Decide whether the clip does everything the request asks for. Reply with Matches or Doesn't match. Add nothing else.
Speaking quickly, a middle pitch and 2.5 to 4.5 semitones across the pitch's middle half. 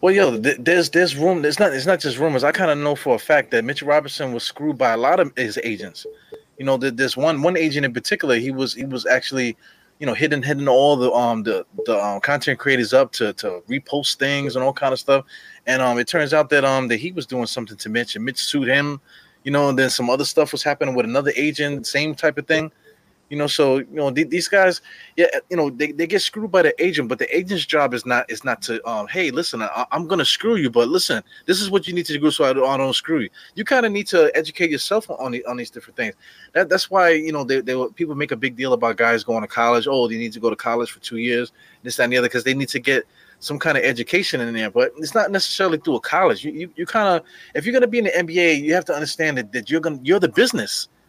Doesn't match